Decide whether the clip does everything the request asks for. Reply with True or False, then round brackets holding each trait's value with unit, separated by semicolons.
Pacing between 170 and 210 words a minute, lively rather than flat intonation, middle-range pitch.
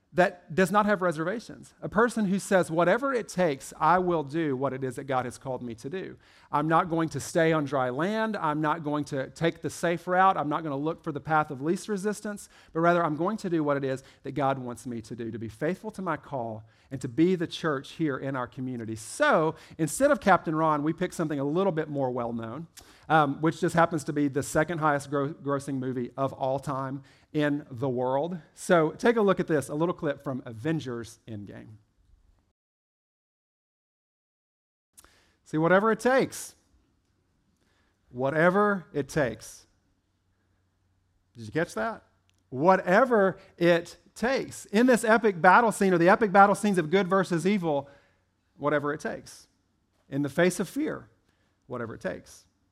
True (190 wpm; 6.2 semitones; 150 Hz)